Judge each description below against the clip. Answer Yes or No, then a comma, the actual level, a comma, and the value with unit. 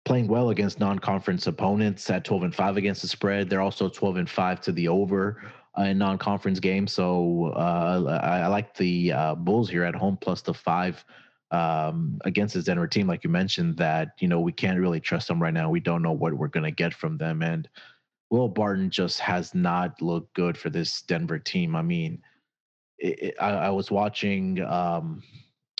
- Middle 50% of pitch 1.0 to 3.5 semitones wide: Yes, average, 3.2 semitones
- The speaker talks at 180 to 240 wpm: Yes, fast, 205 wpm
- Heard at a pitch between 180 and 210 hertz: No, very low, 95 Hz